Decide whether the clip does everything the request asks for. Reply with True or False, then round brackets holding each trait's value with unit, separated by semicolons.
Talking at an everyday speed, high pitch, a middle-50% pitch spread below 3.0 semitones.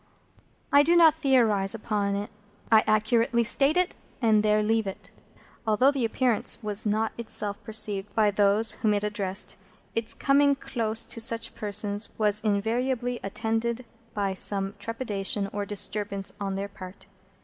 True (150 wpm; 215 Hz; 2.5 semitones)